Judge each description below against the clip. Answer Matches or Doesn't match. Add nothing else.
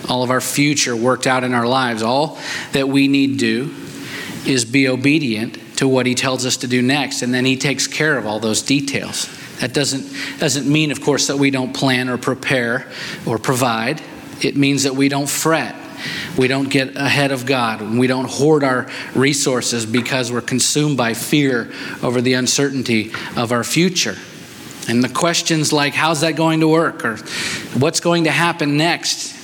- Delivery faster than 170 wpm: Matches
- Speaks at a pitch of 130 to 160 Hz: Matches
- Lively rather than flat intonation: Doesn't match